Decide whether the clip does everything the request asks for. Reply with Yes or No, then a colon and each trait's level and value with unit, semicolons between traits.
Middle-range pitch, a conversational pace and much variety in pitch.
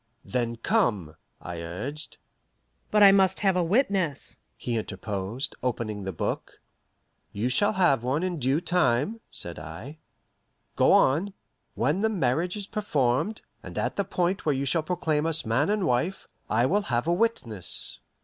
Yes: medium, 150 Hz; average, 160 wpm; wide, 8.1 semitones